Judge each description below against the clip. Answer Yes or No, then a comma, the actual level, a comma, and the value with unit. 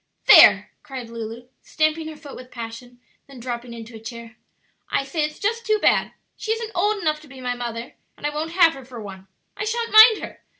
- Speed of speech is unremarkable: No, fast, 215 wpm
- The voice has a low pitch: No, very high, 275 Hz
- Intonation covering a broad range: Yes, wide, 6.3 semitones